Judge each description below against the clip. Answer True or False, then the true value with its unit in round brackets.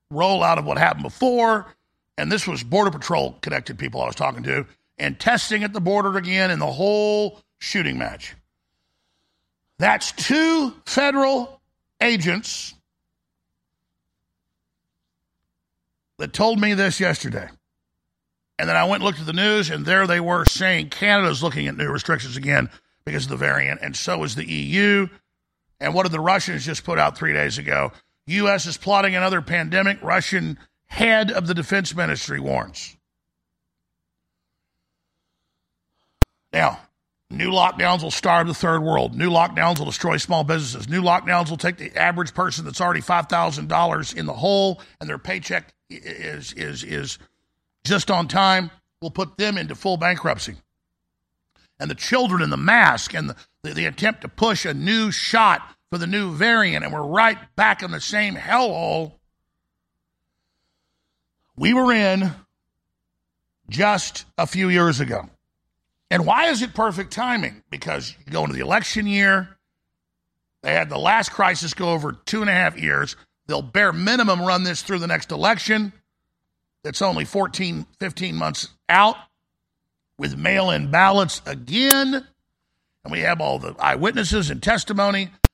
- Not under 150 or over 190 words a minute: True (155 wpm)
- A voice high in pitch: False (175 Hz)